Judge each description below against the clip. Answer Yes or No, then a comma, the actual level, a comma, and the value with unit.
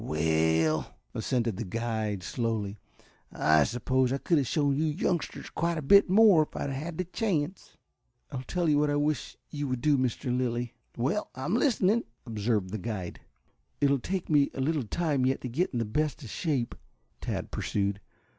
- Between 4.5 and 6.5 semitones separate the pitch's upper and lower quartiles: Yes, wide, 5.6 semitones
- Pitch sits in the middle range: No, low, 130 Hz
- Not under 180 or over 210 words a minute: Yes, average, 185 wpm